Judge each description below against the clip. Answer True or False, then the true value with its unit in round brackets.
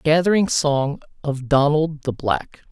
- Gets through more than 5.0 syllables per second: False (3.9 syllables/s)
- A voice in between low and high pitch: True (145 Hz)